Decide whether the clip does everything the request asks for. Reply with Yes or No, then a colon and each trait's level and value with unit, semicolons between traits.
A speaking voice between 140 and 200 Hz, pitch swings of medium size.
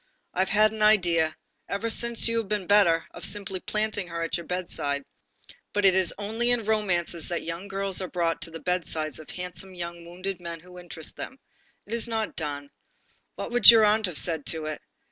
Yes: medium, 185 Hz; average, 4.0 semitones